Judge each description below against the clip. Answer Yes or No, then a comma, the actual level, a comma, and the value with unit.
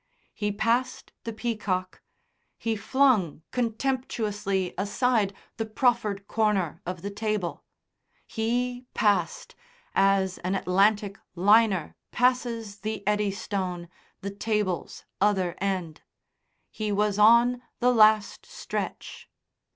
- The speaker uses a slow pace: Yes, slow, 100 wpm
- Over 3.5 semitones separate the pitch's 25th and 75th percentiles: No, average, 2.7 semitones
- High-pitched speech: Yes, high, 210 Hz